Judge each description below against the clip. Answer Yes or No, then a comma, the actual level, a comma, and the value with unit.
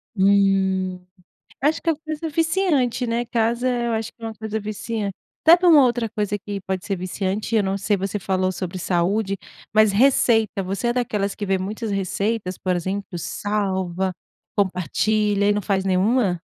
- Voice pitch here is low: No, high, 205 Hz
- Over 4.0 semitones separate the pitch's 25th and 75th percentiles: No, average, 3.3 semitones